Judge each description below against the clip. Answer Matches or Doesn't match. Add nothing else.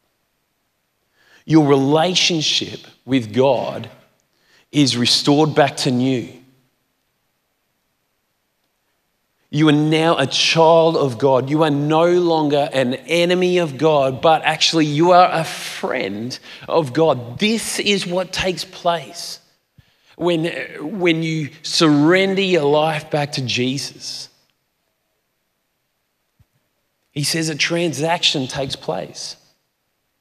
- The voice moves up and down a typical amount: Matches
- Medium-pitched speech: Matches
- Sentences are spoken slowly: Matches